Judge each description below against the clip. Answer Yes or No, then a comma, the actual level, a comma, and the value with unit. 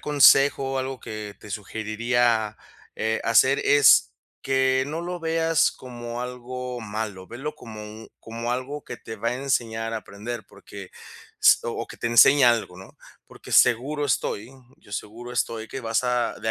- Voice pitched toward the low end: Yes, low, 120 Hz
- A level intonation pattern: No, average, 3.1 semitones